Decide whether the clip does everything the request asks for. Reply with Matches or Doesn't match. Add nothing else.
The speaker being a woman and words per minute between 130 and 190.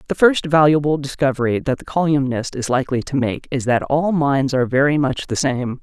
Doesn't match